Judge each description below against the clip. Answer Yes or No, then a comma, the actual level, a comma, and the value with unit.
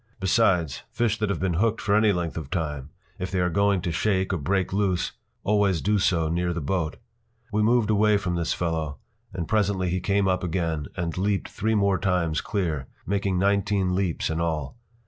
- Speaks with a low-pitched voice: Yes, very low, 95 Hz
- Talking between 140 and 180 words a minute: No, average, 195 wpm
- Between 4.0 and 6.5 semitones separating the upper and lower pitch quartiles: No, average, 3.3 semitones